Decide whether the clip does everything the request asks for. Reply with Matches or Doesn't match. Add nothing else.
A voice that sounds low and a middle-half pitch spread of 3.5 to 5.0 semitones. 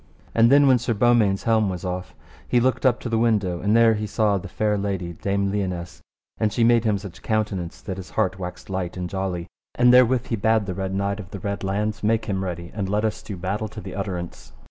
Doesn't match